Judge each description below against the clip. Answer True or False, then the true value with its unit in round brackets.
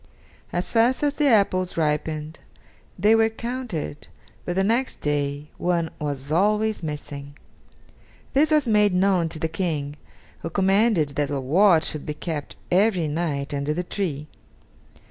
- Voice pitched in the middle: True (175 Hz)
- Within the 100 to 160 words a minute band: True (145 wpm)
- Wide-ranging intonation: True (5.8 semitones)